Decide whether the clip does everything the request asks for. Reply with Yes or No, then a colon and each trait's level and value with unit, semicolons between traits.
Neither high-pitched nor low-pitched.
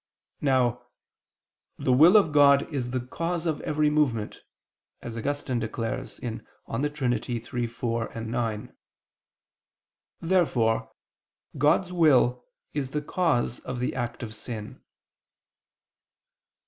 No: low, 125 Hz